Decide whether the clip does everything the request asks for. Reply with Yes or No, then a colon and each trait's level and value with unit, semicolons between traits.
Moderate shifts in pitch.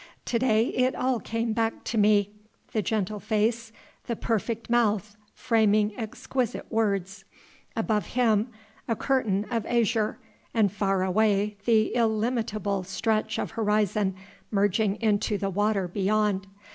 No: narrow, 1.9 semitones